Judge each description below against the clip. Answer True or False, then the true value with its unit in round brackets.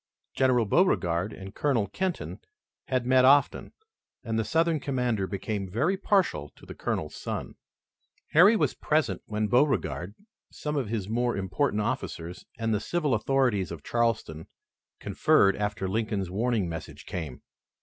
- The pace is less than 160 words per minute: True (140 wpm)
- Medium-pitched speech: False (115 Hz)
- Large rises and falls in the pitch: True (5.7 semitones)